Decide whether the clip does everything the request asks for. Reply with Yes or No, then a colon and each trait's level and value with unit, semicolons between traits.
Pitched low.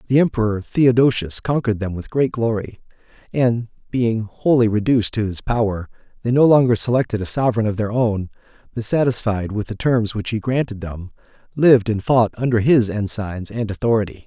Yes: low, 115 Hz